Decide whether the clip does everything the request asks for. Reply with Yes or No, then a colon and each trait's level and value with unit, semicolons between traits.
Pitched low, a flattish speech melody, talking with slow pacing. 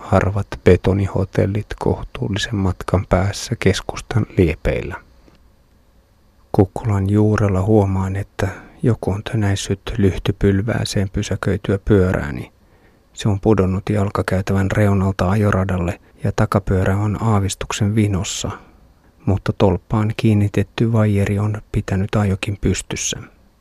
Yes: low, 100 Hz; narrow, 1.9 semitones; slow, 90 wpm